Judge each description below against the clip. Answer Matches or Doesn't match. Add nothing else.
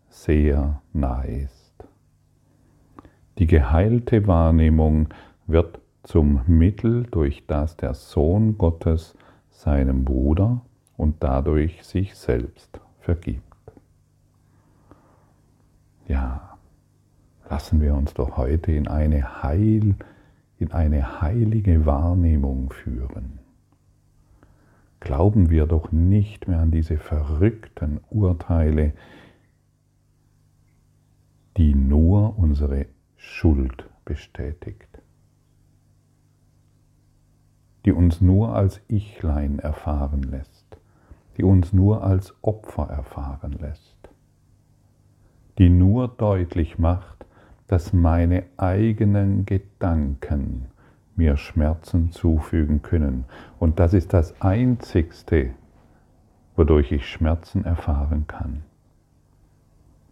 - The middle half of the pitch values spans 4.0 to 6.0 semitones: Matches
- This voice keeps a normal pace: Doesn't match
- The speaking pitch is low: Matches